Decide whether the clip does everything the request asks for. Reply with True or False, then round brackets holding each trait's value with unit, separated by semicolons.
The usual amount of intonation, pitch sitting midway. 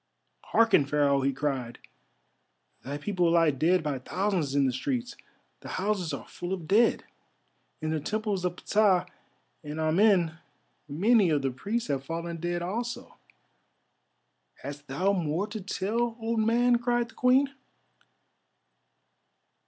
False (6.5 semitones; 175 Hz)